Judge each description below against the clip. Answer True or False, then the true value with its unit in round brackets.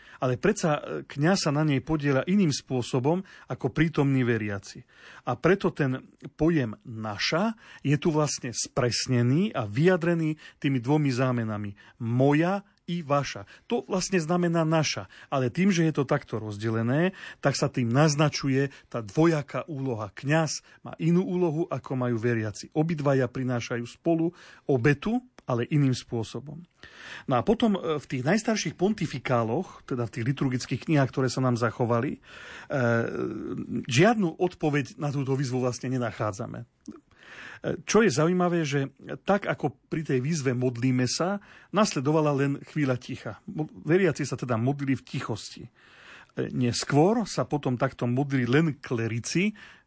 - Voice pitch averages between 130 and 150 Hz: True (140 Hz)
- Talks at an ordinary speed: True (135 wpm)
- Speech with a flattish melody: False (4.5 semitones)